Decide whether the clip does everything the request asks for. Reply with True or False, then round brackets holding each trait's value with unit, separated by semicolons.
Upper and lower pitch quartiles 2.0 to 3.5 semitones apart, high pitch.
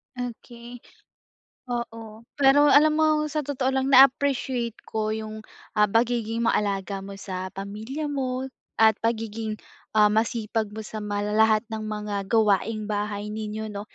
True (2.8 semitones; 220 Hz)